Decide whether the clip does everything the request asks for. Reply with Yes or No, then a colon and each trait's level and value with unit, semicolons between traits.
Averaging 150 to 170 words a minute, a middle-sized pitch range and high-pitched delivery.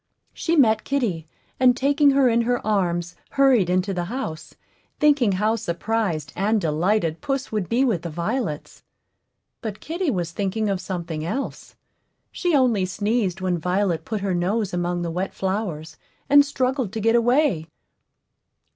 No: average, 155 wpm; wide, 5.9 semitones; high, 205 Hz